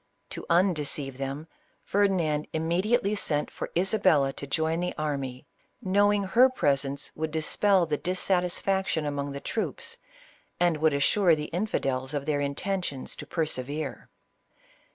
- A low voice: No, medium, 160 Hz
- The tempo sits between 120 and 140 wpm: Yes, slow, 135 wpm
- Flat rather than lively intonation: No, average, 4.8 semitones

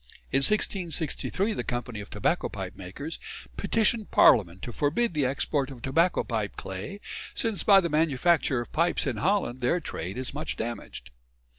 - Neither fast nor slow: Yes, average, 160 wpm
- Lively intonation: Yes, wide, 6.6 semitones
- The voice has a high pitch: No, medium, 140 Hz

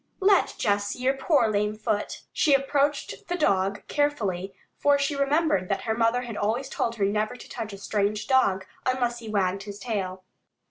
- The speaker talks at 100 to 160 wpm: No, average, 185 wpm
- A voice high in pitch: Yes, high, 225 Hz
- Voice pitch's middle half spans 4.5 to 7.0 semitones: Yes, average, 5.2 semitones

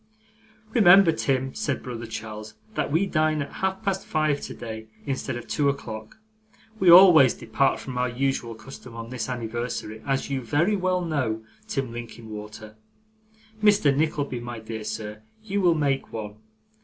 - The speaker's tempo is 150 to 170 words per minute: Yes, average, 155 wpm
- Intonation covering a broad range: Yes, wide, 5.7 semitones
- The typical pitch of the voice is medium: No, low, 130 Hz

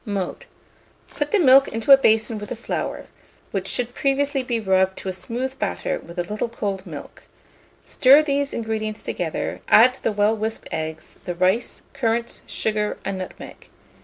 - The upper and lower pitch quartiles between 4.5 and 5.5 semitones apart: Yes, average, 4.9 semitones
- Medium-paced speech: Yes, average, 165 wpm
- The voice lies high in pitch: Yes, high, 220 Hz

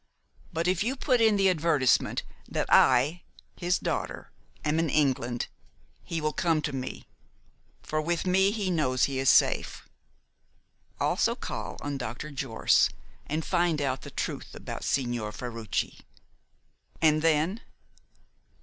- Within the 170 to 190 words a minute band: No, slow, 135 wpm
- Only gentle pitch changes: No, average, 4.8 semitones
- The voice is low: No, medium, 155 Hz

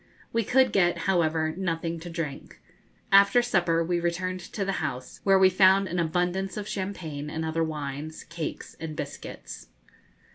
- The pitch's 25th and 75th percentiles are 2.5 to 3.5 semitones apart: Yes, average, 3.1 semitones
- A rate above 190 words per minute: No, average, 155 wpm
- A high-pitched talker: No, medium, 175 Hz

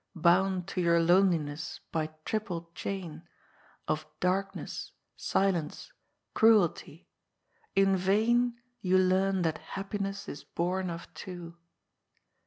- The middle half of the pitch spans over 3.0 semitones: No, narrow, 2.6 semitones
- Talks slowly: Yes, slow, 100 wpm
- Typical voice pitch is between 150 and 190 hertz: Yes, medium, 185 Hz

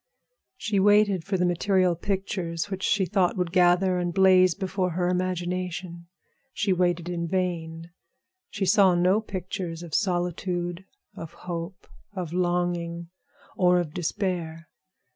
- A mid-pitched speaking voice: Yes, medium, 180 Hz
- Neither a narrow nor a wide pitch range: No, narrow, 1.6 semitones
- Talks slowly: Yes, slow, 130 wpm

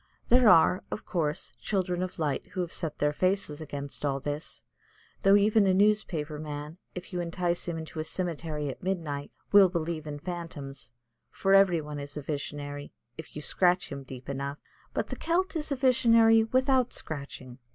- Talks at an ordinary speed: Yes, average, 180 wpm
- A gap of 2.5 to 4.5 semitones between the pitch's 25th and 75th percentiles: No, average, 4.9 semitones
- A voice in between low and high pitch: Yes, medium, 165 Hz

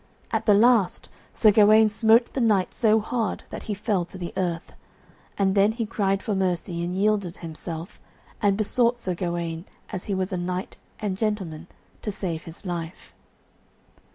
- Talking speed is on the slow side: No, average, 170 wpm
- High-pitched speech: Yes, high, 195 Hz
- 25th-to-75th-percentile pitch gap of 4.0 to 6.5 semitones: No, average, 3.5 semitones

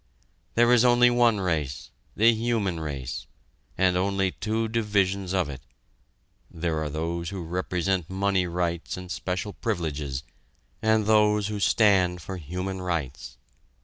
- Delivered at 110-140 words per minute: Yes, slow, 135 wpm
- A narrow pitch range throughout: No, average, 3.9 semitones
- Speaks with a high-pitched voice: No, very low, 95 Hz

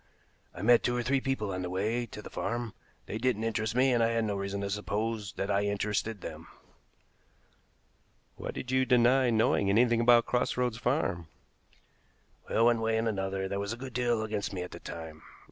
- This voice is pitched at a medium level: No, low, 110 Hz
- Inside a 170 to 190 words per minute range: No, average, 200 wpm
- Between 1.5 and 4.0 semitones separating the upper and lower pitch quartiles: Yes, average, 3.2 semitones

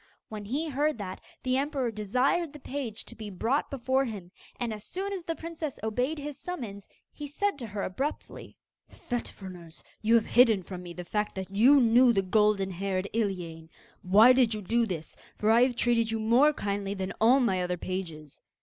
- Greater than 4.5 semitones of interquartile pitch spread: Yes, average, 5.2 semitones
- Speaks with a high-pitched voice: Yes, high, 225 Hz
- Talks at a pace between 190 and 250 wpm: Yes, average, 195 wpm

